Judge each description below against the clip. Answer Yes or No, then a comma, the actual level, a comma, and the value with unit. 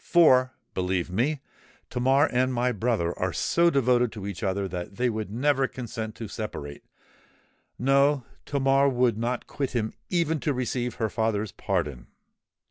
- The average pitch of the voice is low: Yes, low, 120 Hz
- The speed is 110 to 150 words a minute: Yes, average, 140 wpm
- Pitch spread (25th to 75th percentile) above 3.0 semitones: Yes, average, 4.1 semitones